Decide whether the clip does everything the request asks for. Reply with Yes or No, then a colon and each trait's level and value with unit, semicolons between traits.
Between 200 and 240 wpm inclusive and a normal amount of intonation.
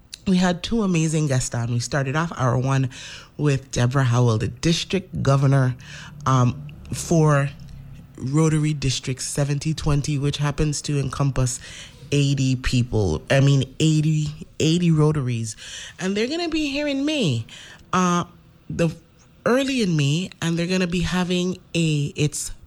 No: average, 140 wpm; average, 3.9 semitones